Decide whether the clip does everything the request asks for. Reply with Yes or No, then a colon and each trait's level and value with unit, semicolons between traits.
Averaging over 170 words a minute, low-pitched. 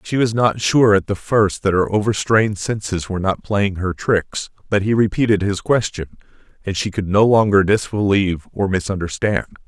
Yes: average, 180 wpm; low, 100 Hz